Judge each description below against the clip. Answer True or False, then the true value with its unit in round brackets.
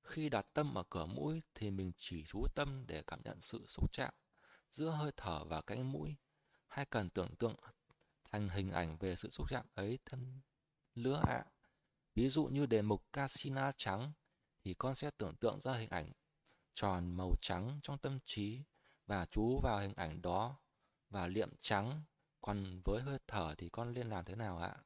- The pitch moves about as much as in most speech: False (6.4 semitones)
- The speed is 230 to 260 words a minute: False (190 wpm)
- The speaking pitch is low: True (115 Hz)